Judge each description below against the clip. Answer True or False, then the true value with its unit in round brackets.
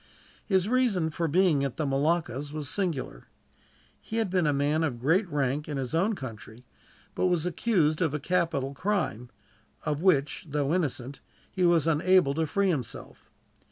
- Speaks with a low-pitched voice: False (155 Hz)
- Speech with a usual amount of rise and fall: True (4.6 semitones)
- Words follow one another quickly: False (165 wpm)